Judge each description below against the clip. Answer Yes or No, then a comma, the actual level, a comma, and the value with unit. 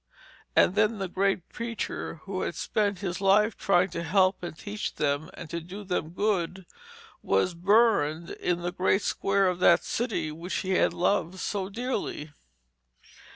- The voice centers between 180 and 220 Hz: Yes, medium, 185 Hz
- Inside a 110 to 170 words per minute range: Yes, average, 160 wpm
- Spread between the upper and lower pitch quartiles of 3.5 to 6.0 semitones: No, average, 2.9 semitones